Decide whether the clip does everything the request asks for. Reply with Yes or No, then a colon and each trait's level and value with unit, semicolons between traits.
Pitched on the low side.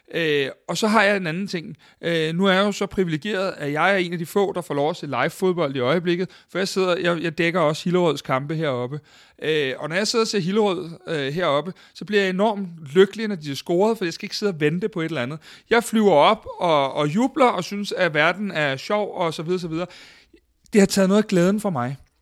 No: medium, 180 Hz